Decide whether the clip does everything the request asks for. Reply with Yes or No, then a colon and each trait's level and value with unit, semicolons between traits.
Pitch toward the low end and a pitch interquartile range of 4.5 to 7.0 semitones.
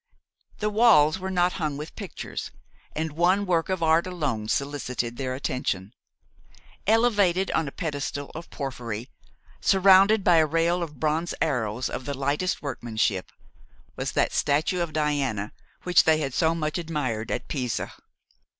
No: medium, 155 Hz; average, 4.8 semitones